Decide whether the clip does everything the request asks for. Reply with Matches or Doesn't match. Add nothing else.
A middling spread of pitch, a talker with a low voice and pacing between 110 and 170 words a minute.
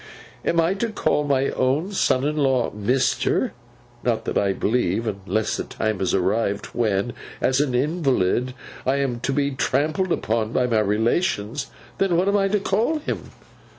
Doesn't match